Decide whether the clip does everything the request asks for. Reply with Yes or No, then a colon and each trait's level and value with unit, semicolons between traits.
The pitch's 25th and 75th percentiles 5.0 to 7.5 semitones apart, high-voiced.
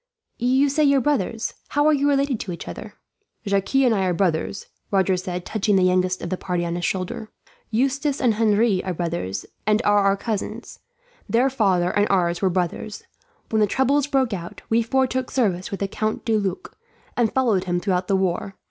Yes: wide, 5.4 semitones; high, 205 Hz